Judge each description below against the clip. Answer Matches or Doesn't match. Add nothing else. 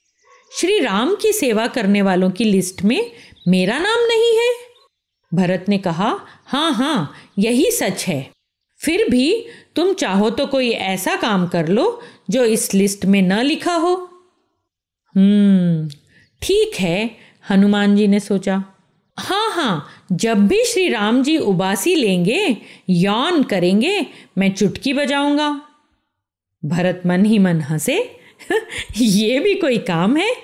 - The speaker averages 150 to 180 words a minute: Doesn't match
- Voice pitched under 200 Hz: Doesn't match